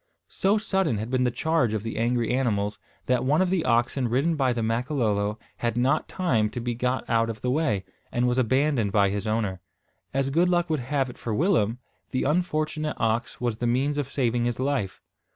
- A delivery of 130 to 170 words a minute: No, fast, 205 wpm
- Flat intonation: No, average, 4.3 semitones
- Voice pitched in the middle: No, low, 125 Hz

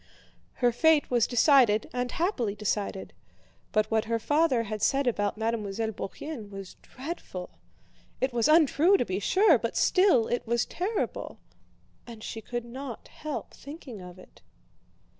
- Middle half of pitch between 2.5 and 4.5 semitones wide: No, average, 5.1 semitones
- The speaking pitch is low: No, high, 240 Hz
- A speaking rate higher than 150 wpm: No, average, 145 wpm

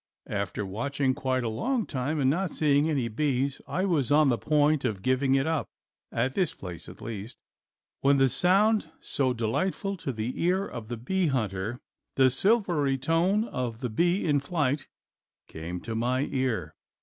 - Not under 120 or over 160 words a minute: No, average, 175 wpm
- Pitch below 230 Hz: Yes, low, 135 Hz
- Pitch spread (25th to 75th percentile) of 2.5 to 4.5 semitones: No, wide, 5.5 semitones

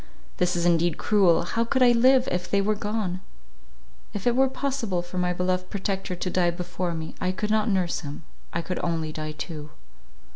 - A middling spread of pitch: Yes, average, 3.5 semitones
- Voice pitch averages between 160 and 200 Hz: Yes, medium, 185 Hz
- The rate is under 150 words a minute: No, average, 195 wpm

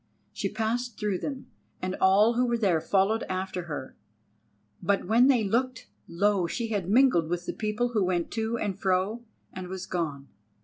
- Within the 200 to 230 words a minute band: No, average, 175 wpm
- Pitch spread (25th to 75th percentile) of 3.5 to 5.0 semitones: Yes, average, 3.9 semitones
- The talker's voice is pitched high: Yes, high, 200 Hz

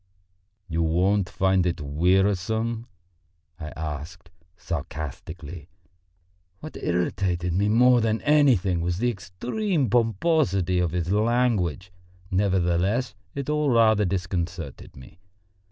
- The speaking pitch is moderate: No, very low, 95 Hz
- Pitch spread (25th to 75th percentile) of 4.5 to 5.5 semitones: Yes, average, 4.8 semitones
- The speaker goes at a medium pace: No, slow, 105 wpm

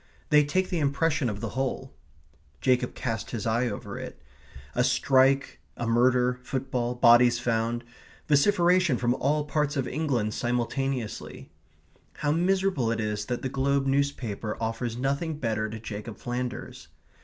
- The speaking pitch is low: Yes, low, 125 Hz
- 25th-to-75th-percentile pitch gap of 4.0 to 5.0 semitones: No, average, 3.2 semitones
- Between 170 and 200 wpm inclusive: No, average, 145 wpm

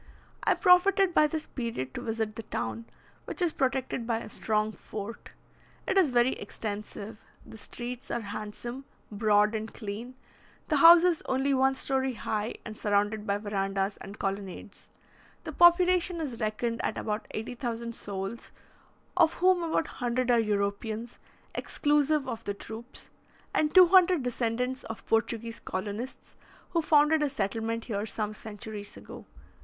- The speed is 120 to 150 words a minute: Yes, average, 145 wpm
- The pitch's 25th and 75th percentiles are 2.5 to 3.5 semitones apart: No, average, 4.8 semitones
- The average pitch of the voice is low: No, high, 230 Hz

